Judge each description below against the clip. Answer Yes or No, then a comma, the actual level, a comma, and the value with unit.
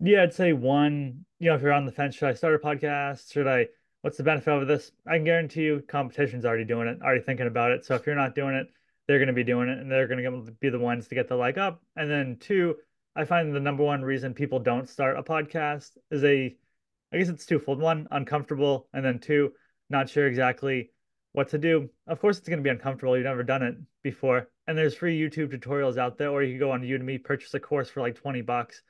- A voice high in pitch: No, medium, 140 Hz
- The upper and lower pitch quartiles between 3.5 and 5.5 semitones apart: No, average, 2.7 semitones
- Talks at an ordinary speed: No, fast, 255 wpm